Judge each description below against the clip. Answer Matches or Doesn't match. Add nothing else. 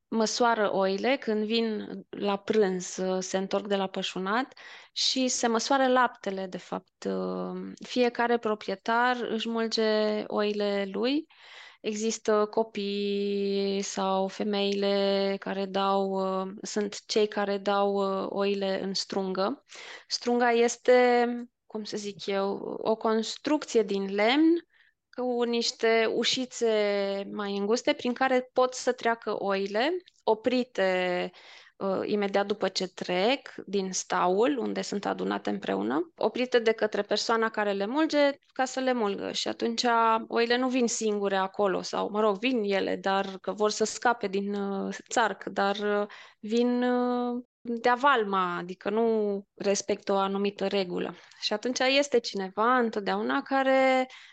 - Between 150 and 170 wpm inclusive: Doesn't match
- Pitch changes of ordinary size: Matches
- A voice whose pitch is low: Doesn't match